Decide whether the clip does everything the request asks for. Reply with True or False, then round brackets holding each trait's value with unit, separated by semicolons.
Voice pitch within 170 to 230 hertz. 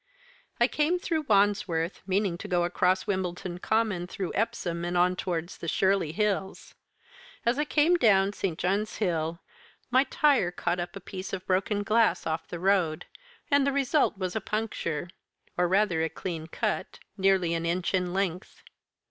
True (190 Hz)